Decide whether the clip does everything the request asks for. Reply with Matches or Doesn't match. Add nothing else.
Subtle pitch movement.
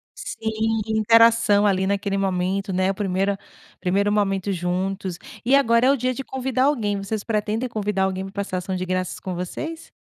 Doesn't match